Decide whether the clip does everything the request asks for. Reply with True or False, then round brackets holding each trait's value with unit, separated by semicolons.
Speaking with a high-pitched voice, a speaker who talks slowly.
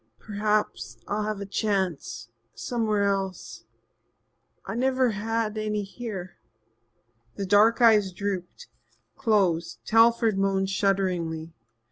True (205 Hz; 100 wpm)